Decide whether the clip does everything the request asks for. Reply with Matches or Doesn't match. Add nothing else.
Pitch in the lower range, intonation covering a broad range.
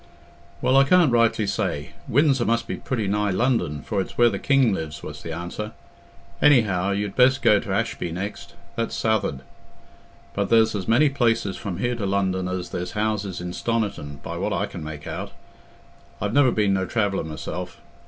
Doesn't match